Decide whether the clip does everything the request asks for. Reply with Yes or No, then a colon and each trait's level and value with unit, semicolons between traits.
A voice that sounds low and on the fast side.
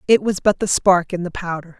No: medium, 185 Hz; fast, 265 wpm